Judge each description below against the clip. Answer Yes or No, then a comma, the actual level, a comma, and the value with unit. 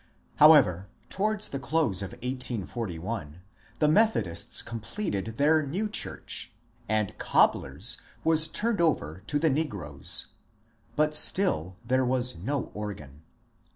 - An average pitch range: No, wide, 8.4 semitones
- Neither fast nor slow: No, slow, 125 wpm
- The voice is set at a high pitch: No, low, 125 Hz